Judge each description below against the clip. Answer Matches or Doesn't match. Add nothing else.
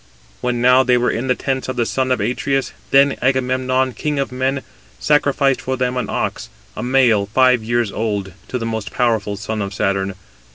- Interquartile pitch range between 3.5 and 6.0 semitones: Doesn't match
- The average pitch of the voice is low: Matches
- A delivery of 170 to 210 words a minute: Matches